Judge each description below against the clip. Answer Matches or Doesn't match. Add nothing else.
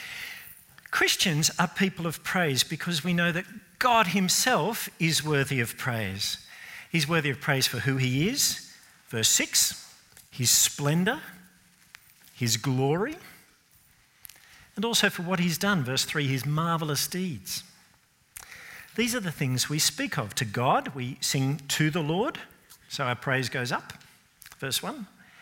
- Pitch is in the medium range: Matches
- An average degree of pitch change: Doesn't match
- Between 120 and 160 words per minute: Matches